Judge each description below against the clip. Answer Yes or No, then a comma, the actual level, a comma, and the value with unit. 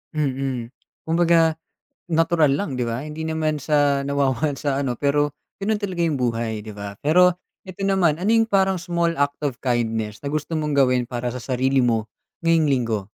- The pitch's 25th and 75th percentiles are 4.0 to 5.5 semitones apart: Yes, average, 4.8 semitones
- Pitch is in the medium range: Yes, medium, 145 Hz